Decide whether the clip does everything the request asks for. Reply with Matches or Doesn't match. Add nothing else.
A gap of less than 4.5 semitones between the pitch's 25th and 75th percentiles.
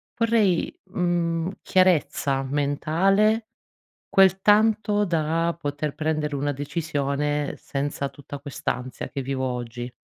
Doesn't match